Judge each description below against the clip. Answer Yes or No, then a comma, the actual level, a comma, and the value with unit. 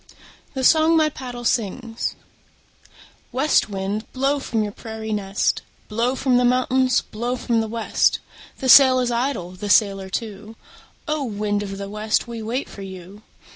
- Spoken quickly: No, average, 160 wpm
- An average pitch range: Yes, average, 3.7 semitones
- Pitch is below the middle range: No, high, 230 Hz